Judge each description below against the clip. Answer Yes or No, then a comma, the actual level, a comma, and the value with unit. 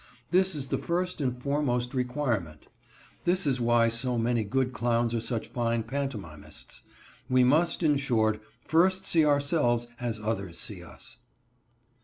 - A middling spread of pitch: Yes, average, 4.0 semitones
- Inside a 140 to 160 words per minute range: Yes, average, 145 wpm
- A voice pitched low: Yes, low, 125 Hz